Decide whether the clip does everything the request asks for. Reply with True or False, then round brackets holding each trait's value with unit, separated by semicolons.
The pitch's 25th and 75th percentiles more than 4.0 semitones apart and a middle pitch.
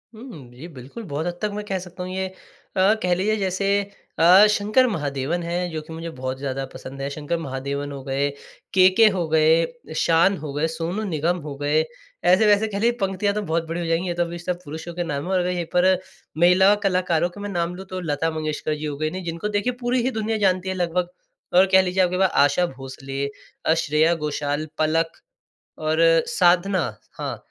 False (3.5 semitones; 170 Hz)